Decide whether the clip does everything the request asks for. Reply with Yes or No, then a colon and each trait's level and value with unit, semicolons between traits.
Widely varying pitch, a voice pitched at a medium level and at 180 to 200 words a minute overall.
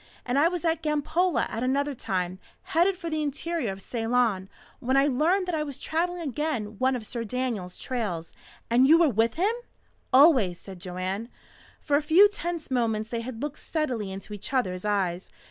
No: wide, 6.8 semitones; very high, 255 Hz; average, 185 wpm